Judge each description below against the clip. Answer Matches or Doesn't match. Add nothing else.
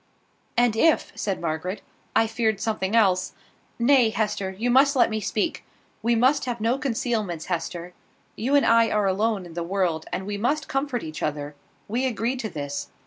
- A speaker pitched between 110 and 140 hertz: Doesn't match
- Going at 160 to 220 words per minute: Matches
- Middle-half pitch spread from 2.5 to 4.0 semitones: Doesn't match